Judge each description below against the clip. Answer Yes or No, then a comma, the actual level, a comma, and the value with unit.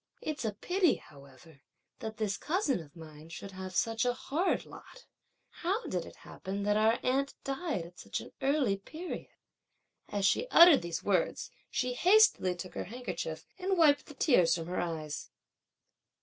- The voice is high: Yes, high, 220 Hz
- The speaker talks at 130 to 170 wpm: Yes, average, 165 wpm